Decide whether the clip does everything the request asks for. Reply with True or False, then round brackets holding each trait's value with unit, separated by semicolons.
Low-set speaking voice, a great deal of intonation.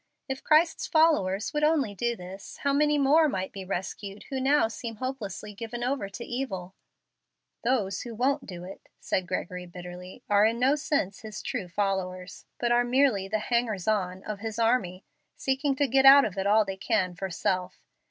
False (220 Hz; 5.7 semitones)